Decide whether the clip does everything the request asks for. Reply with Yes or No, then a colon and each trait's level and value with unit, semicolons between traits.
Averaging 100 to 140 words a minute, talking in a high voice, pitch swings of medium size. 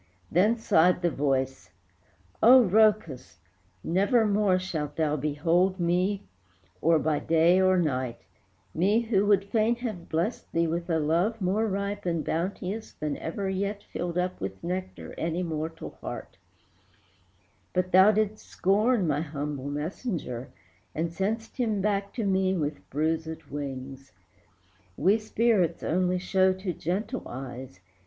No: slow, 135 wpm; medium, 180 Hz; average, 4.3 semitones